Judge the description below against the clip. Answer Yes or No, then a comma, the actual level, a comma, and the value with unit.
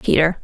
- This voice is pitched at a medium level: Yes, medium, 160 Hz